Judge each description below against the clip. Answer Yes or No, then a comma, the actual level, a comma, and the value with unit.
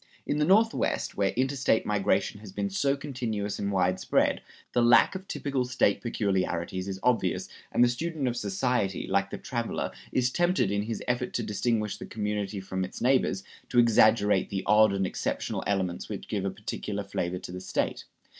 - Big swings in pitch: No, average, 4.2 semitones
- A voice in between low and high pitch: No, low, 105 Hz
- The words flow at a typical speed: Yes, average, 180 wpm